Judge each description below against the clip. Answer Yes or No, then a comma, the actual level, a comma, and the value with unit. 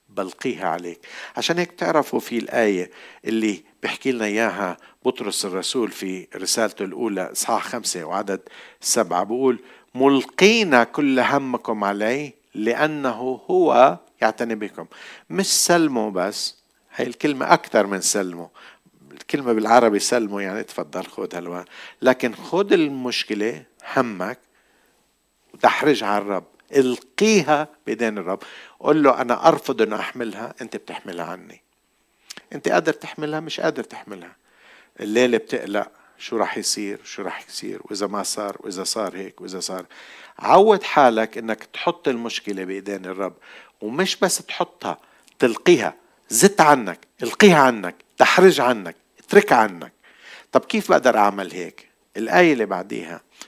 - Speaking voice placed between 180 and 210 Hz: No, low, 120 Hz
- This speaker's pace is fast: No, average, 125 wpm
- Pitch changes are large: Yes, wide, 6.6 semitones